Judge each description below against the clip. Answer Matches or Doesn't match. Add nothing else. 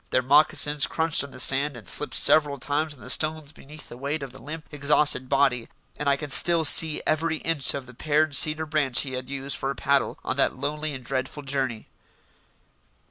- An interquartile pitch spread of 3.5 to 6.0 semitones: Doesn't match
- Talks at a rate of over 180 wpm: Matches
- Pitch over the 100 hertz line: Matches